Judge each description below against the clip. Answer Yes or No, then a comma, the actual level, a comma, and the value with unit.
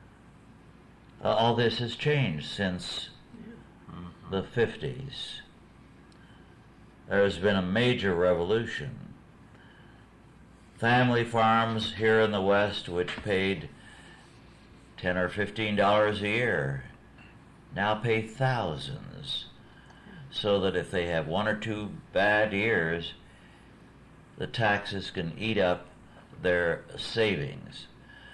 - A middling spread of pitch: Yes, average, 4.0 semitones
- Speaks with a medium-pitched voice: No, low, 105 Hz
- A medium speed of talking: No, slow, 100 wpm